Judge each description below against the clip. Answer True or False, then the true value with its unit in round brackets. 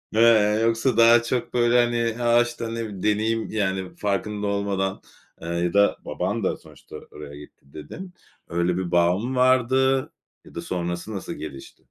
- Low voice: True (105 Hz)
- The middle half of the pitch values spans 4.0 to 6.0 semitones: True (4.3 semitones)